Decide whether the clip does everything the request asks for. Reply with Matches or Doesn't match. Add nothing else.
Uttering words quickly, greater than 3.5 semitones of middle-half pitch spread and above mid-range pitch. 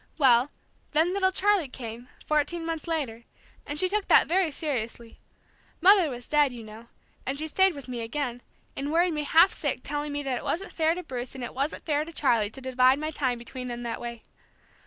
Matches